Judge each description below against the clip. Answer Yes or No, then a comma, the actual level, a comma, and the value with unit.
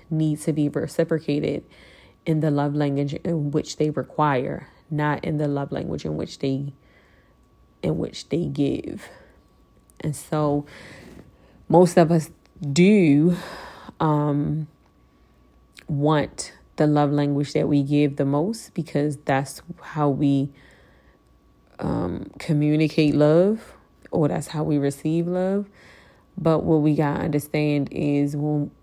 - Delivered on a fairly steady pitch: Yes, narrow, 1.8 semitones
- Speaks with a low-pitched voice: No, medium, 150 Hz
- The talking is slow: Yes, slow, 125 wpm